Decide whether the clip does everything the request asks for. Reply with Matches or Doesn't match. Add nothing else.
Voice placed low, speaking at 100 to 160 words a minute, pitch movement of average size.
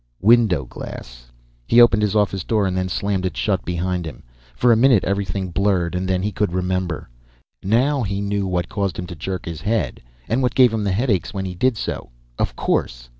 Doesn't match